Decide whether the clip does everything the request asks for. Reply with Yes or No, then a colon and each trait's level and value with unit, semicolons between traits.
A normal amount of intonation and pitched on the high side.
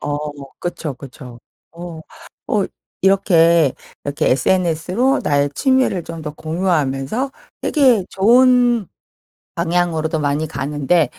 No: average, 4.8 semitones; medium, 170 Hz